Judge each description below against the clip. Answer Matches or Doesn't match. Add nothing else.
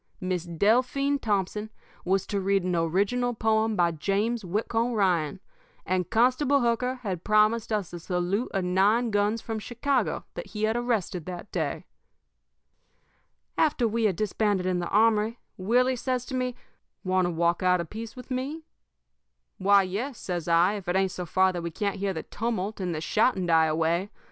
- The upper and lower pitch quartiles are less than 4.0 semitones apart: Doesn't match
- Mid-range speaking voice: Doesn't match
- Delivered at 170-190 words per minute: Matches